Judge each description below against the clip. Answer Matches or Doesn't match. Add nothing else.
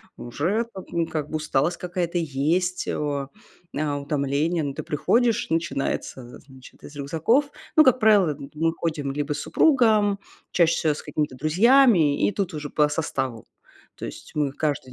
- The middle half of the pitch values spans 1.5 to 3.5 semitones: Doesn't match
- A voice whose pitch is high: Doesn't match